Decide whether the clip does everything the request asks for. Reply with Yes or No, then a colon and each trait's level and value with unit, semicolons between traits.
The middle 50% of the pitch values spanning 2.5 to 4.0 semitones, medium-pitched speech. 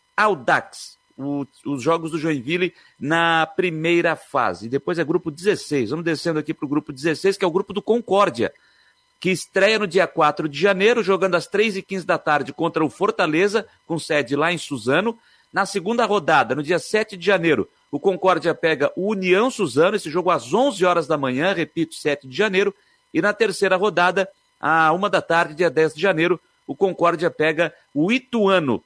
Yes: average, 3.7 semitones; medium, 175 Hz